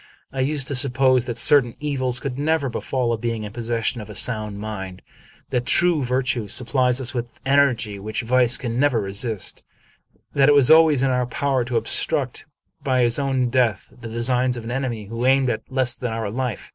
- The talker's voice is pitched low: Yes, low, 125 Hz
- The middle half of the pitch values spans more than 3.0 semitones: No, narrow, 2.5 semitones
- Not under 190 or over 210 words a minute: Yes, fast, 205 wpm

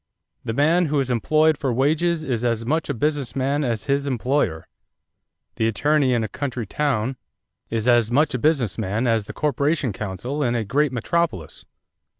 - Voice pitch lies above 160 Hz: No, low, 130 Hz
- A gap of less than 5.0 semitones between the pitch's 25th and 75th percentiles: Yes, average, 4.6 semitones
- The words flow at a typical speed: Yes, average, 175 wpm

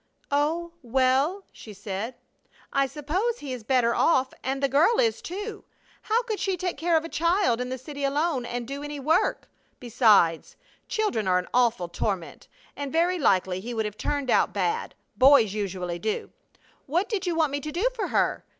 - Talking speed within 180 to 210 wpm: Yes, average, 185 wpm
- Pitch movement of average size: No, wide, 6.6 semitones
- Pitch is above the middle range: Yes, very high, 275 Hz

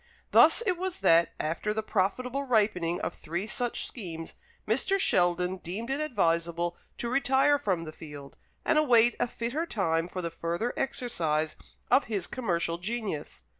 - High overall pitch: Yes, high, 205 Hz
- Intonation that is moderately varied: No, wide, 6.8 semitones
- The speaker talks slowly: No, average, 155 wpm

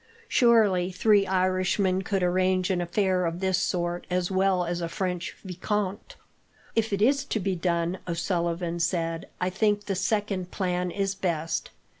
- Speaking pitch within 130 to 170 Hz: No, medium, 185 Hz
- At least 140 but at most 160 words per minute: Yes, average, 155 wpm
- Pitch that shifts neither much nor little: No, narrow, 2.0 semitones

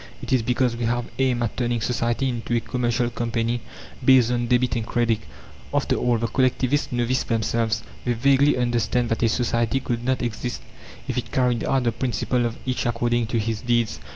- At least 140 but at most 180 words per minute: No, average, 200 wpm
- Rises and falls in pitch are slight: Yes, narrow, 1.3 semitones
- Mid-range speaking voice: No, low, 120 Hz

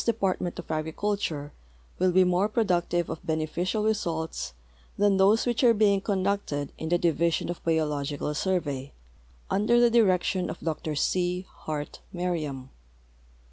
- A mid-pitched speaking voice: Yes, medium, 175 Hz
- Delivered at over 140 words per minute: No, slow, 135 wpm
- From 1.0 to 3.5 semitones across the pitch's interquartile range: No, average, 4.3 semitones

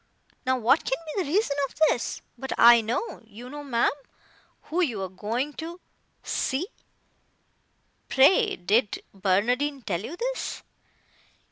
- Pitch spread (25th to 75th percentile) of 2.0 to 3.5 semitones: No, average, 5.0 semitones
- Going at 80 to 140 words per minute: Yes, slow, 135 wpm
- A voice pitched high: Yes, very high, 260 Hz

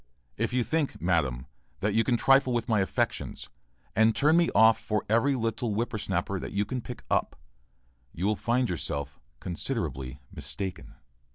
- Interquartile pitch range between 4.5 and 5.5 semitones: Yes, average, 5.1 semitones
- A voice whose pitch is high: No, low, 110 Hz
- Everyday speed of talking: Yes, average, 165 wpm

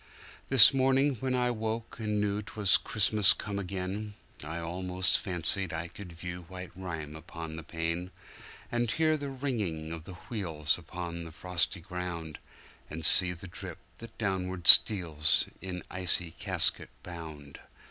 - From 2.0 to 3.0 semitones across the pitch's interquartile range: No, average, 4.2 semitones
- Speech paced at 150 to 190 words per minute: No, slow, 135 wpm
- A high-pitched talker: No, very low, 90 Hz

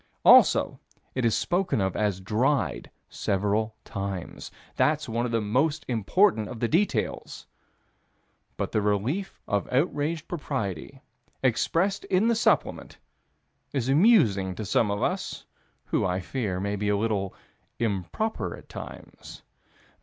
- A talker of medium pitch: No, low, 115 Hz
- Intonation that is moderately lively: No, wide, 6.8 semitones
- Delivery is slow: Yes, slow, 130 wpm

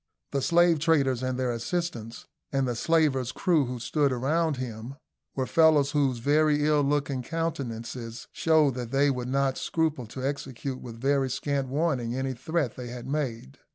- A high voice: No, low, 135 Hz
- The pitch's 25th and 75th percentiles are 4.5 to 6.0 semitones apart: No, average, 3.3 semitones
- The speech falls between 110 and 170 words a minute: Yes, average, 165 wpm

